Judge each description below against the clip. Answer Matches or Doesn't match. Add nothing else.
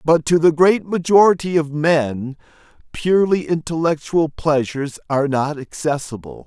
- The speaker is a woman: Doesn't match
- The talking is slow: Matches